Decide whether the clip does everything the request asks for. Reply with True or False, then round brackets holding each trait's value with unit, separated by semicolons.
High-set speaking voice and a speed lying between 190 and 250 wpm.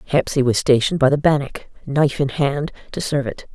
False (140 Hz; 205 wpm)